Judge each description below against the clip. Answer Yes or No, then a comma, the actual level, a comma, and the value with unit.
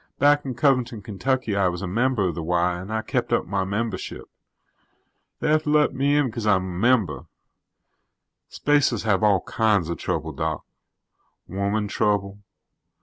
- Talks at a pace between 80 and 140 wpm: No, average, 165 wpm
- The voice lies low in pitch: Yes, low, 105 Hz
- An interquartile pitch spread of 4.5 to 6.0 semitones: Yes, wide, 5.5 semitones